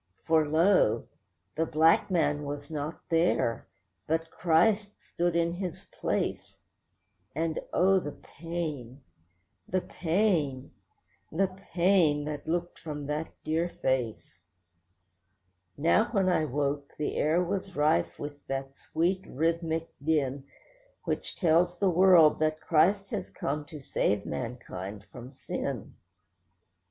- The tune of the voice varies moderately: Yes, average, 3.4 semitones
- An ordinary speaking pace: No, slow, 120 wpm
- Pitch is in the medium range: Yes, medium, 160 Hz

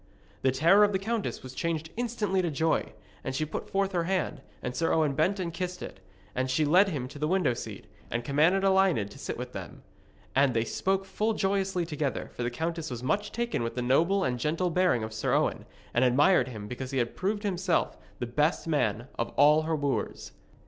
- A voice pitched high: No, medium, 160 Hz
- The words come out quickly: Yes, fast, 215 wpm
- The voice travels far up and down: Yes, wide, 6.7 semitones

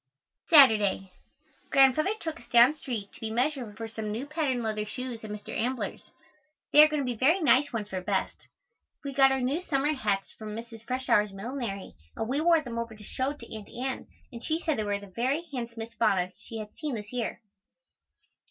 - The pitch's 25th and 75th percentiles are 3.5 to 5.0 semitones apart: Yes, average, 4.4 semitones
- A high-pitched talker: Yes, high, 240 Hz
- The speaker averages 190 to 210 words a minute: Yes, average, 200 wpm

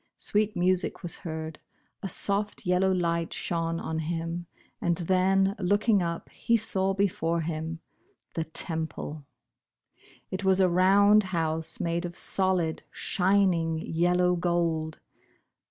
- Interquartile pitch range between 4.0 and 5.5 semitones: No, narrow, 2.6 semitones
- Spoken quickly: No, slow, 135 wpm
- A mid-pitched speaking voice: Yes, medium, 175 Hz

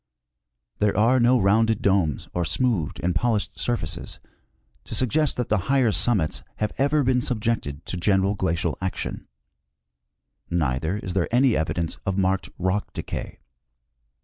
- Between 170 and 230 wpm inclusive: No, average, 145 wpm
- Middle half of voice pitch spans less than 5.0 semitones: No, wide, 5.5 semitones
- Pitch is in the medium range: No, low, 100 Hz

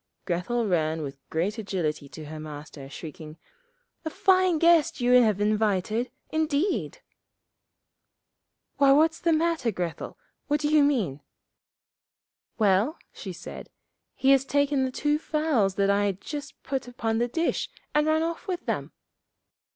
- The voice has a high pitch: Yes, high, 240 Hz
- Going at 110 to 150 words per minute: Yes, average, 145 wpm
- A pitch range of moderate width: No, wide, 8.4 semitones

